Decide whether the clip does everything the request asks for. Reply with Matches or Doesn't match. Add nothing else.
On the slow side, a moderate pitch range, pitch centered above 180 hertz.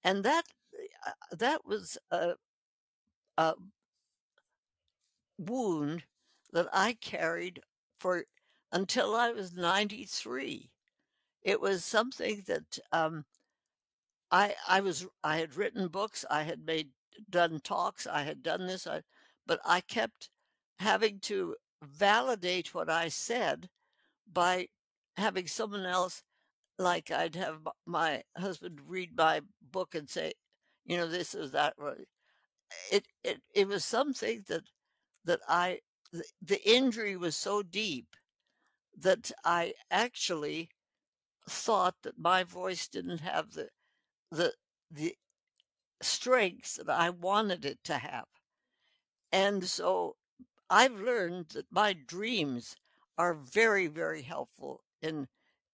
Matches